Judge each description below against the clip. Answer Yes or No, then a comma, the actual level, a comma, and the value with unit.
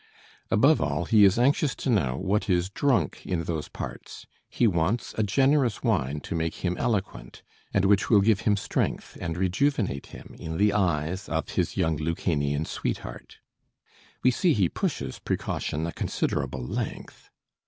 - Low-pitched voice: Yes, very low, 95 Hz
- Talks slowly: No, average, 160 wpm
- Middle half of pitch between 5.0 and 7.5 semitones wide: Yes, wide, 5.4 semitones